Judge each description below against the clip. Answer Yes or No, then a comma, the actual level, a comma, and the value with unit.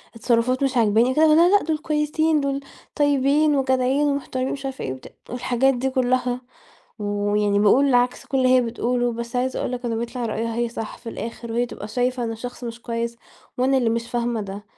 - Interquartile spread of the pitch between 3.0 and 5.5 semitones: No, narrow, 2.5 semitones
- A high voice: Yes, high, 245 Hz